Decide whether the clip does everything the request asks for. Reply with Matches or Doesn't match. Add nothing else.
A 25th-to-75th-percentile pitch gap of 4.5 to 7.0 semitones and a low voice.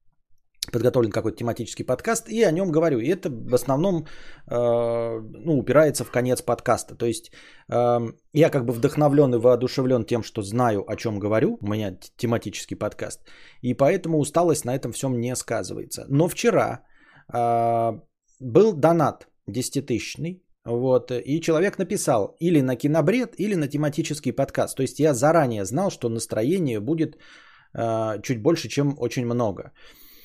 Matches